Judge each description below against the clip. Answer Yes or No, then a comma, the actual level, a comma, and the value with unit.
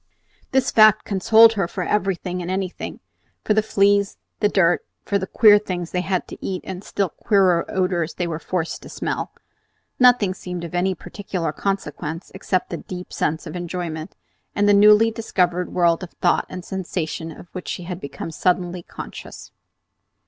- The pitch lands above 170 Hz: Yes, medium, 185 Hz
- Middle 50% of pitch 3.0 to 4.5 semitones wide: No, narrow, 2.5 semitones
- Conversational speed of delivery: Yes, average, 175 wpm